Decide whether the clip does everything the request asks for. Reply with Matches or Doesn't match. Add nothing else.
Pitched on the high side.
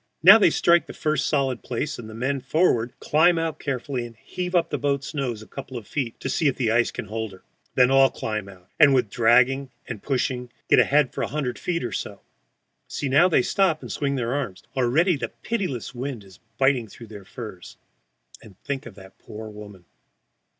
Doesn't match